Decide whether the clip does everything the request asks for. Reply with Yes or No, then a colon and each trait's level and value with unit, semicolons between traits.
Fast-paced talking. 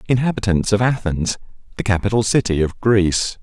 No: average, 140 wpm